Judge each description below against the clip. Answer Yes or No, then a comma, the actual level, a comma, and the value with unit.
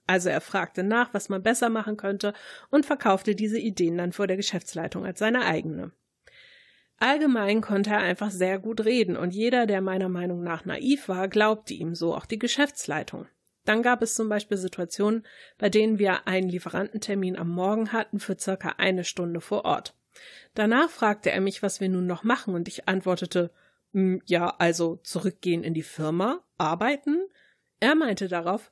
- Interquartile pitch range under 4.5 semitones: Yes, average, 3.4 semitones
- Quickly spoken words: No, average, 175 wpm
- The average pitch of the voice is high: Yes, high, 200 Hz